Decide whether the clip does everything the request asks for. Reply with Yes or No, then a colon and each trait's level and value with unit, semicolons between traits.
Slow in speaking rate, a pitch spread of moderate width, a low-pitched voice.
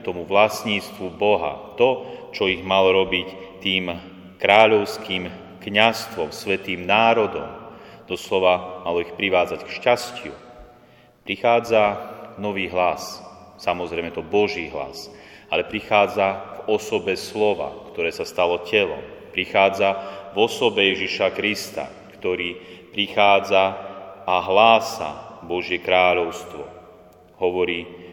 Yes: slow, 100 wpm; average, 3.0 semitones; very low, 95 Hz